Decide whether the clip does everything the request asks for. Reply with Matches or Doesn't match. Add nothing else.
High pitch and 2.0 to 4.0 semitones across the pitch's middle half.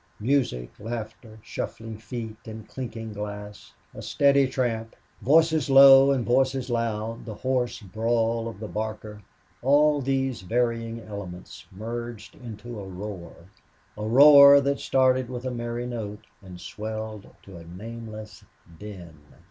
Doesn't match